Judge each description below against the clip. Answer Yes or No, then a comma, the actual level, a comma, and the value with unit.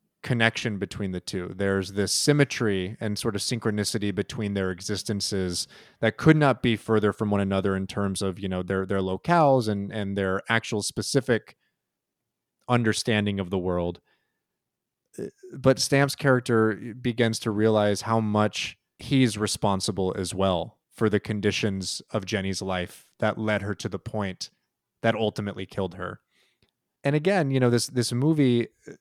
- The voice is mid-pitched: No, low, 105 Hz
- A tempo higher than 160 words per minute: No, average, 155 wpm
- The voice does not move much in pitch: No, average, 3.3 semitones